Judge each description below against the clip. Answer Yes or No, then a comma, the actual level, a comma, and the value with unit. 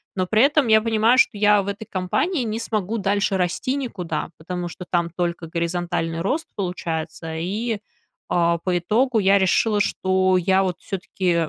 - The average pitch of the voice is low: No, high, 190 Hz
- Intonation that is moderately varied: Yes, average, 3.8 semitones